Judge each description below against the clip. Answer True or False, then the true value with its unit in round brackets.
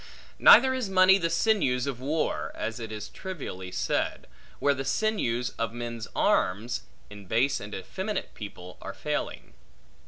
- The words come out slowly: False (150 wpm)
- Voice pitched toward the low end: True (125 Hz)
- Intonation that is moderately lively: False (8.9 semitones)